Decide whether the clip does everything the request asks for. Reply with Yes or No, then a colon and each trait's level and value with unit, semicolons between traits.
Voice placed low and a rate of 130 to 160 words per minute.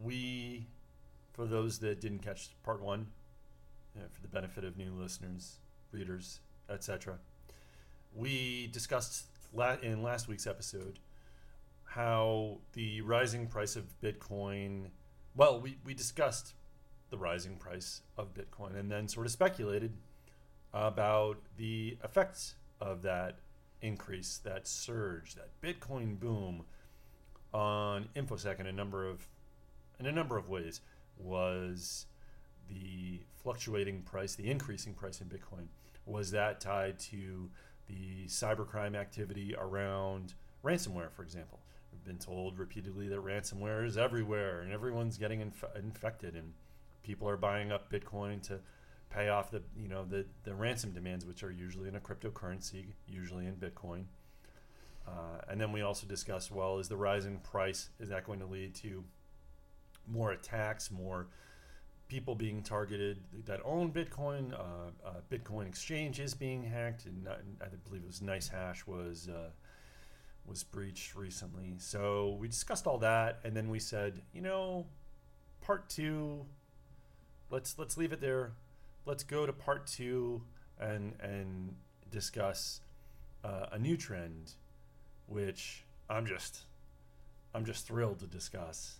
Yes: low, 100 Hz; average, 140 wpm